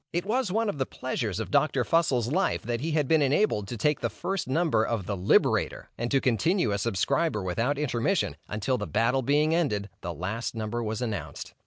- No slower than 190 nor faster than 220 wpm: Yes, fast, 205 wpm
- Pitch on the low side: Yes, low, 125 Hz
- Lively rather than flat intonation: Yes, wide, 6.5 semitones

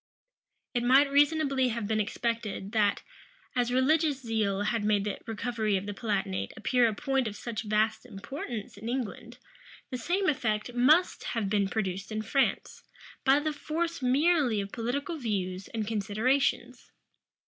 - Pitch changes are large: No, average, 4.4 semitones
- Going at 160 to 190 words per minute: No, average, 150 wpm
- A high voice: Yes, high, 230 Hz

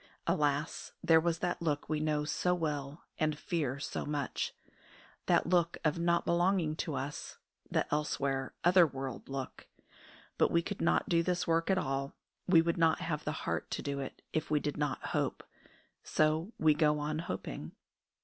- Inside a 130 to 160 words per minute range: No, average, 175 wpm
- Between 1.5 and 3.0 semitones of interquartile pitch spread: Yes, narrow, 2.5 semitones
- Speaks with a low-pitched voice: No, medium, 155 Hz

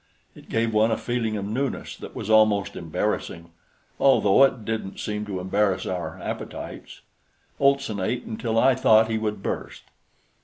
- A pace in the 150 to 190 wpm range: Yes, average, 155 wpm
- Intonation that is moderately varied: No, narrow, 2.3 semitones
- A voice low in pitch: Yes, low, 110 Hz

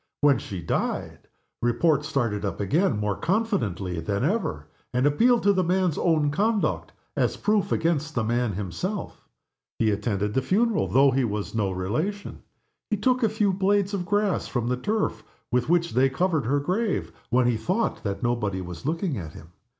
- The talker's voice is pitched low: No, medium, 145 Hz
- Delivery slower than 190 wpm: Yes, average, 175 wpm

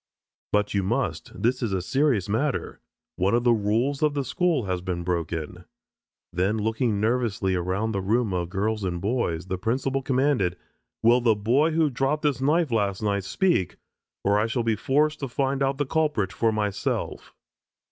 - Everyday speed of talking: Yes, average, 180 wpm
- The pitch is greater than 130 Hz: No, low, 110 Hz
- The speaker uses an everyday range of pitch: No, wide, 5.7 semitones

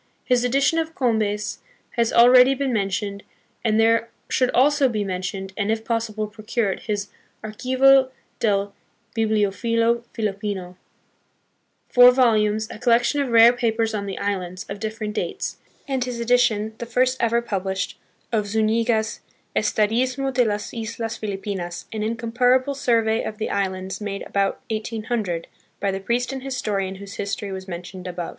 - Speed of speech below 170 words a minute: Yes, average, 150 wpm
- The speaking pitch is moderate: No, high, 220 Hz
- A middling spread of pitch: Yes, average, 3.3 semitones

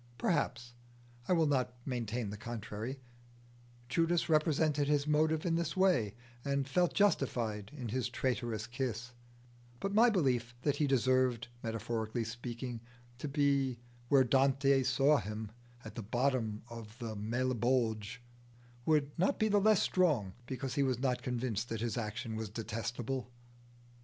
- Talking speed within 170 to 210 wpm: No, average, 140 wpm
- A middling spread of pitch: Yes, average, 3.8 semitones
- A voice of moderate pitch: No, low, 125 Hz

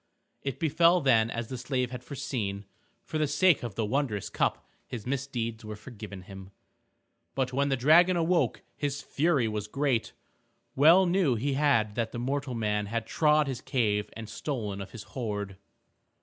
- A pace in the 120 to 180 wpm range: Yes, average, 165 wpm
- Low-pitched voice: Yes, low, 125 Hz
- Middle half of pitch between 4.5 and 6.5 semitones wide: Yes, average, 4.9 semitones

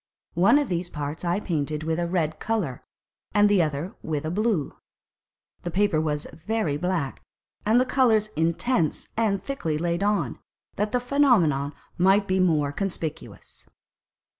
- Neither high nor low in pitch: Yes, medium, 175 Hz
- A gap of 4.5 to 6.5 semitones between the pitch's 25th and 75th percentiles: Yes, average, 5.1 semitones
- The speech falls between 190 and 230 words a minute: No, average, 150 wpm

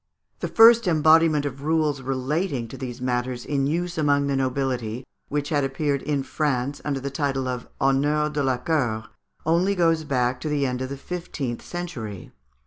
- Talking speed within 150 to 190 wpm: Yes, average, 175 wpm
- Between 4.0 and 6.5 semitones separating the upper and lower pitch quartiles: No, average, 3.2 semitones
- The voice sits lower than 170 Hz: Yes, medium, 140 Hz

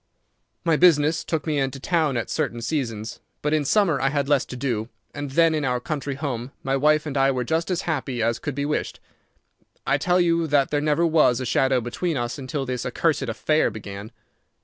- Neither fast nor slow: No, fast, 210 wpm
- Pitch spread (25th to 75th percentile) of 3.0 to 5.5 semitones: Yes, average, 3.6 semitones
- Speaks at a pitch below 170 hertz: Yes, medium, 140 Hz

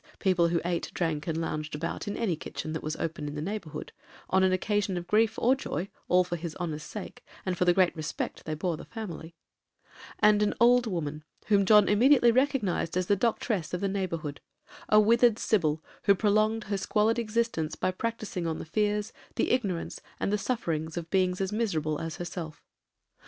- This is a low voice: No, medium, 185 Hz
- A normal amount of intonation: Yes, average, 4.5 semitones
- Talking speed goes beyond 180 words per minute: Yes, average, 190 wpm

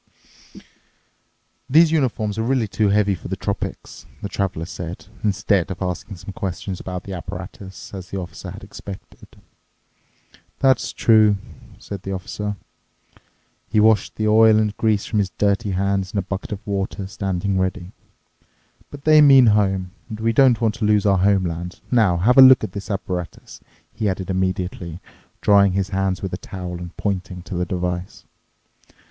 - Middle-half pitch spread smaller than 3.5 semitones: Yes, narrow, 2.5 semitones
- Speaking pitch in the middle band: No, low, 100 Hz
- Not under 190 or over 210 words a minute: No, average, 165 wpm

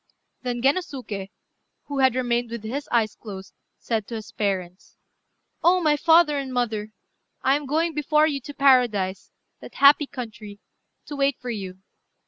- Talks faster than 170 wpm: No, average, 155 wpm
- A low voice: No, very high, 250 Hz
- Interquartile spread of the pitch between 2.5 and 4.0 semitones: No, average, 5.0 semitones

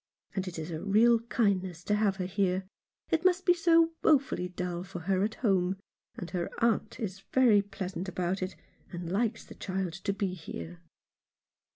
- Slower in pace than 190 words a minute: Yes, average, 180 wpm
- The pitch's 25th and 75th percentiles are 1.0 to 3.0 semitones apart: No, average, 3.4 semitones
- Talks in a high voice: Yes, high, 195 Hz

